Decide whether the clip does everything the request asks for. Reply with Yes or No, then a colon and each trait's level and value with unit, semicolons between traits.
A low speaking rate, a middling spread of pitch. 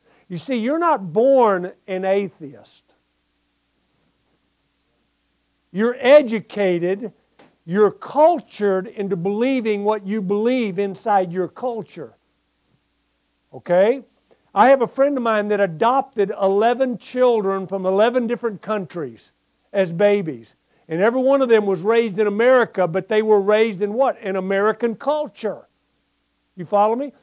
Yes: slow, 125 wpm; average, 3.9 semitones